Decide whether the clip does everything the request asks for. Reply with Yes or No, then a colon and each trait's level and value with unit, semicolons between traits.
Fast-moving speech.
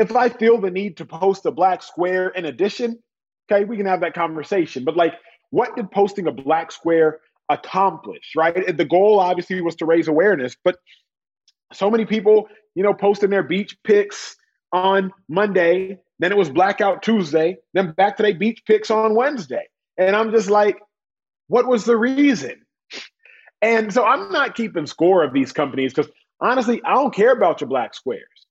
No: average, 180 wpm